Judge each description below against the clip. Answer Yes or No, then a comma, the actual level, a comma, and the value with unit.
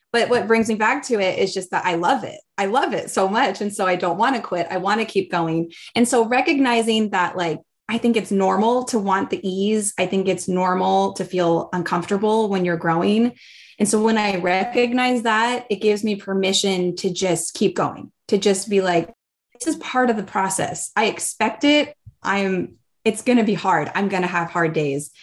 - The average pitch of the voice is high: Yes, high, 195 Hz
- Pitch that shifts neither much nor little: Yes, average, 3.7 semitones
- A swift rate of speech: Yes, fast, 220 wpm